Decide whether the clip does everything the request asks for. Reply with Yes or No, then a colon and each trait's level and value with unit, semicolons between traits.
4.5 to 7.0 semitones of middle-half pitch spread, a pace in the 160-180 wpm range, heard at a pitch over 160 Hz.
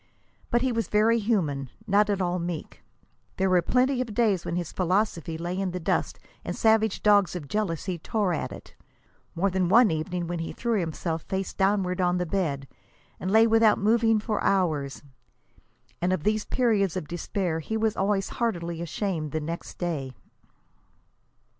No: average, 4.0 semitones; average, 170 wpm; medium, 185 Hz